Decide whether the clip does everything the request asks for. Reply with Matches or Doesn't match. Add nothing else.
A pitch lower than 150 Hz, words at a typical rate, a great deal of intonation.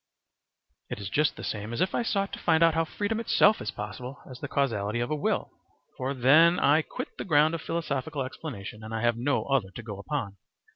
Doesn't match